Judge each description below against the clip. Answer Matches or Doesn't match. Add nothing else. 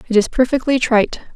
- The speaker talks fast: Doesn't match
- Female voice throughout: Matches